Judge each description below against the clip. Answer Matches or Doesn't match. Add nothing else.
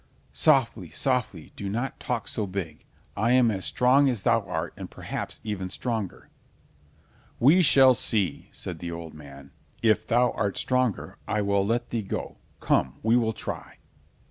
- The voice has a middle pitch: Doesn't match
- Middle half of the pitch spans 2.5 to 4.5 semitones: Doesn't match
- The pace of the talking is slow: Doesn't match